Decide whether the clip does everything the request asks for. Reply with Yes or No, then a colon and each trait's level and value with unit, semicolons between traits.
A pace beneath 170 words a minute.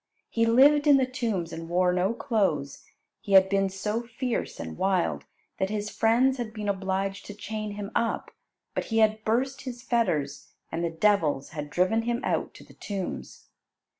No: average, 180 wpm